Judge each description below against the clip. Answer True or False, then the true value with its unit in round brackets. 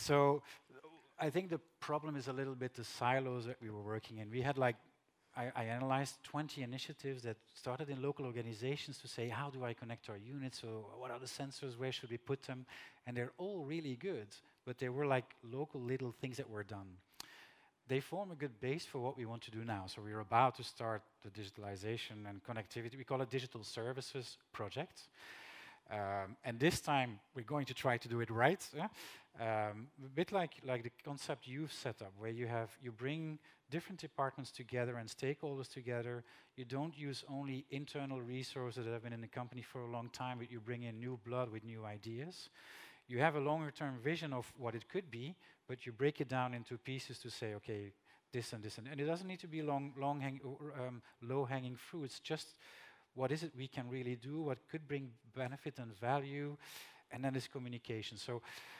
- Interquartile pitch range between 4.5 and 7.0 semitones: False (3.0 semitones)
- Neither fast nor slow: False (215 wpm)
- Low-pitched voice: True (130 Hz)